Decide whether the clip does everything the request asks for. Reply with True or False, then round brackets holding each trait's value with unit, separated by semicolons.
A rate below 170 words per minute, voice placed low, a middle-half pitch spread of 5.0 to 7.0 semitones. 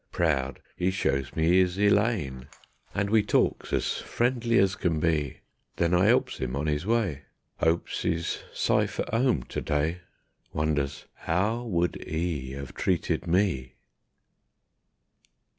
True (135 wpm; 85 Hz; 5.6 semitones)